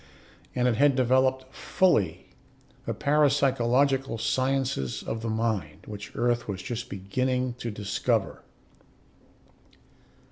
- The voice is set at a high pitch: No, low, 125 Hz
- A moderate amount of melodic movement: Yes, average, 3.3 semitones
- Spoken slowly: Yes, slow, 105 wpm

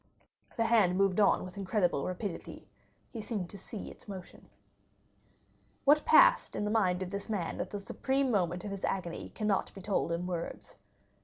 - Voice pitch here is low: No, high, 195 Hz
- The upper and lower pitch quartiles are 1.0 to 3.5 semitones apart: Yes, average, 3.1 semitones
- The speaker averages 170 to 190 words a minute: Yes, average, 175 wpm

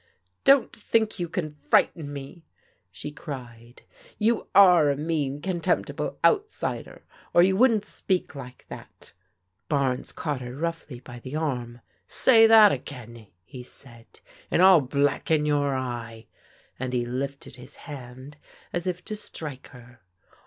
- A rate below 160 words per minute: Yes, average, 140 wpm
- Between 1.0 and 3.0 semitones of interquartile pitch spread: No, wide, 5.6 semitones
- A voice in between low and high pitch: Yes, medium, 145 Hz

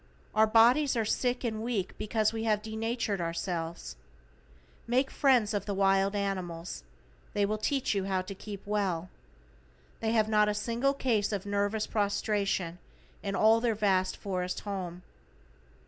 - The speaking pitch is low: No, high, 210 Hz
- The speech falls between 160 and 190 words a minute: No, average, 150 wpm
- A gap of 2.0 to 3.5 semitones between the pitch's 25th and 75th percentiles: Yes, narrow, 2.6 semitones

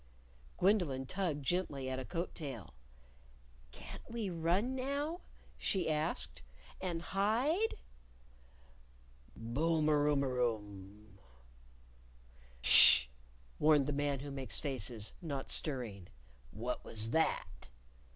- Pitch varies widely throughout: Yes, wide, 6.7 semitones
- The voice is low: No, medium, 145 Hz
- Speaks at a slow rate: Yes, slow, 105 wpm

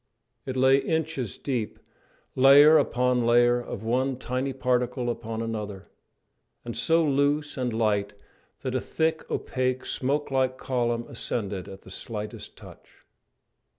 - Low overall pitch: Yes, low, 125 Hz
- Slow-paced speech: Yes, slow, 130 wpm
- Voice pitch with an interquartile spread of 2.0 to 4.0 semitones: Yes, average, 2.8 semitones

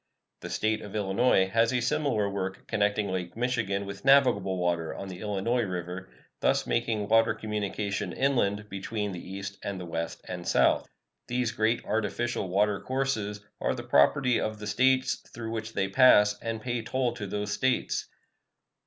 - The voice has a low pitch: Yes, low, 105 Hz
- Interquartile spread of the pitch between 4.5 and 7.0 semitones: No, average, 3.3 semitones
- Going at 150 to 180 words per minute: Yes, average, 165 wpm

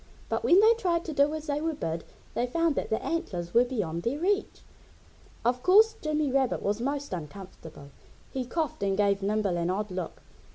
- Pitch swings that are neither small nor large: No, wide, 8.2 semitones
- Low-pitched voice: No, very high, 250 Hz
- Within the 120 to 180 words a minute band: No, average, 195 wpm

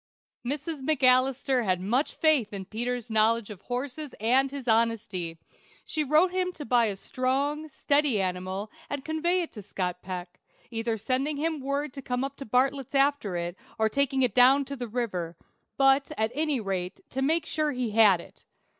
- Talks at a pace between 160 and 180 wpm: Yes, average, 175 wpm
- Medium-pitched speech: No, very high, 255 Hz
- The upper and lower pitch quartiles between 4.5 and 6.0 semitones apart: Yes, average, 4.8 semitones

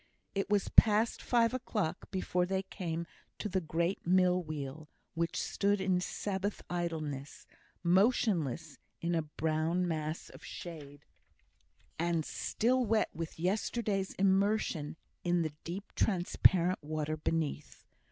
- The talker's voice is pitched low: No, medium, 175 Hz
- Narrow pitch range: No, average, 3.7 semitones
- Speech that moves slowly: Yes, slow, 125 wpm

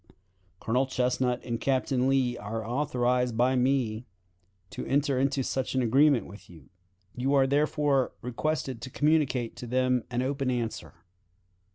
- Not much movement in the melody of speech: Yes, narrow, 2.0 semitones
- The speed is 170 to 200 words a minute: No, average, 145 wpm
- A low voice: Yes, low, 130 Hz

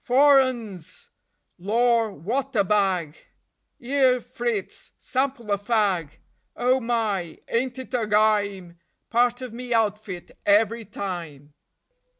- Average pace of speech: No, slow, 115 wpm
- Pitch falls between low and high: No, high, 225 Hz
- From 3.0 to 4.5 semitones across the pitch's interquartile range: Yes, average, 4.0 semitones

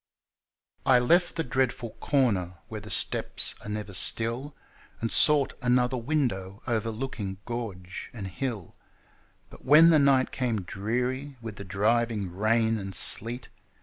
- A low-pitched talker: Yes, low, 115 Hz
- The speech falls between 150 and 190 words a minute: No, slow, 135 wpm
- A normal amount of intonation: Yes, average, 4.2 semitones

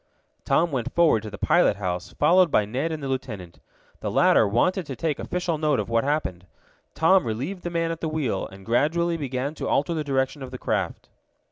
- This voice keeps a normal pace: No, fast, 210 wpm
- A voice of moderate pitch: Yes, medium, 145 Hz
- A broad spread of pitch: Yes, wide, 6.4 semitones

